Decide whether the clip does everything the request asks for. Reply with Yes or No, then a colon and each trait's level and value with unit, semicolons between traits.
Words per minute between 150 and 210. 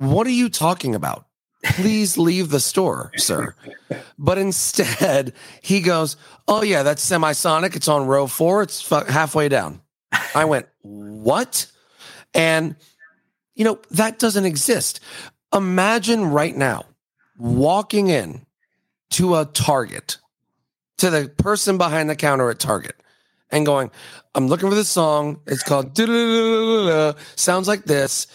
No: slow, 135 wpm